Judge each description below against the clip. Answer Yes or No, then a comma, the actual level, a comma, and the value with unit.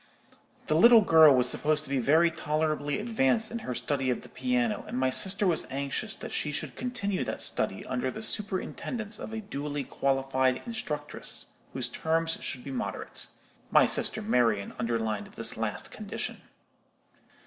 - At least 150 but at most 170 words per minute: Yes, average, 160 wpm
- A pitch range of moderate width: No, wide, 7.8 semitones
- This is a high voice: No, medium, 150 Hz